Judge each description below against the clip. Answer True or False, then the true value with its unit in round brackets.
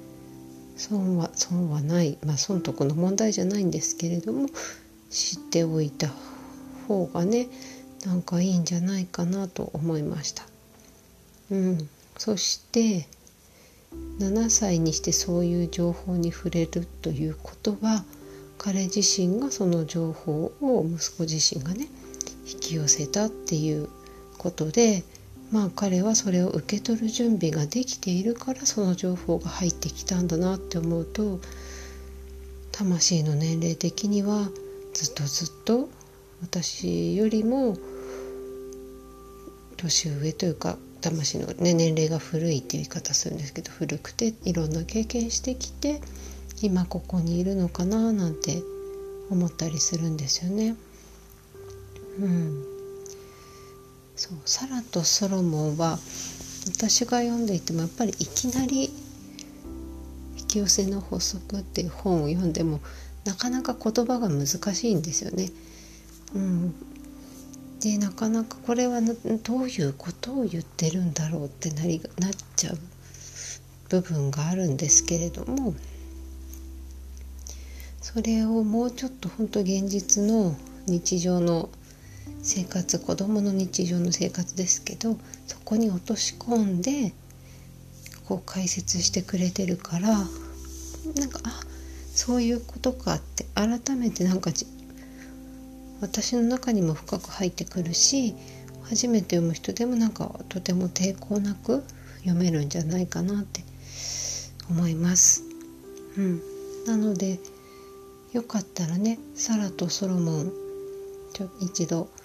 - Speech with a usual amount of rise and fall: False (5.8 semitones)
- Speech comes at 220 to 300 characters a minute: True (250 characters per minute)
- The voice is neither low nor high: True (180 Hz)